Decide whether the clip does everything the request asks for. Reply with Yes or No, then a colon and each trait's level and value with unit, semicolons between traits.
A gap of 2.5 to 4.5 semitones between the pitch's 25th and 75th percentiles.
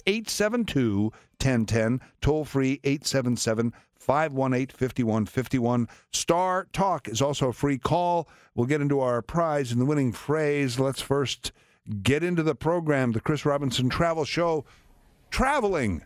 Yes: average, 4.2 semitones